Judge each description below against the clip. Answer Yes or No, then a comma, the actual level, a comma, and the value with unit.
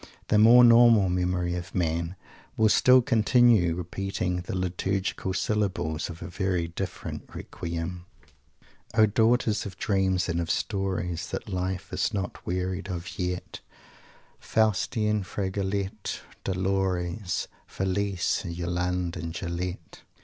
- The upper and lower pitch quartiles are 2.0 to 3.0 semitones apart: Yes, narrow, 2.5 semitones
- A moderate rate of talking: No, slow, 120 wpm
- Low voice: Yes, very low, 95 Hz